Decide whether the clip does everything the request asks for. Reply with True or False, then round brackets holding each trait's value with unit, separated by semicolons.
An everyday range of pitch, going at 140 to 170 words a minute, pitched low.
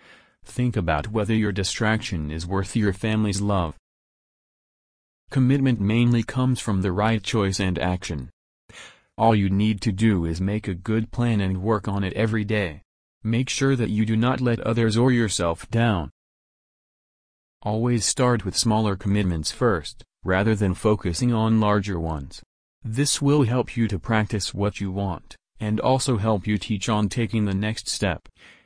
True (3.3 semitones; 160 wpm; 105 Hz)